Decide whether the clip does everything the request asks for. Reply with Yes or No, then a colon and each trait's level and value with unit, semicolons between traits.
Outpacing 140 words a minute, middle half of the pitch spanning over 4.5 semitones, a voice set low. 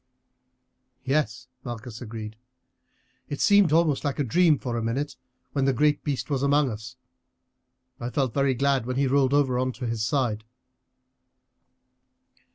No: average, 150 wpm; average, 3.2 semitones; low, 130 Hz